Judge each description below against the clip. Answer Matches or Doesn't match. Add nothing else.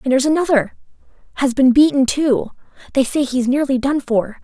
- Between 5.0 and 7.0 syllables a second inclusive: Matches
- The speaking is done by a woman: Matches